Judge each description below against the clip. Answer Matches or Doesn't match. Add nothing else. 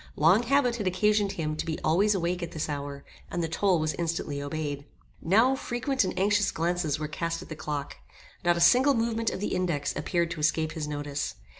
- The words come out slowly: Doesn't match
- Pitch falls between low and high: Matches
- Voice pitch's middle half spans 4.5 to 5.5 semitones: Matches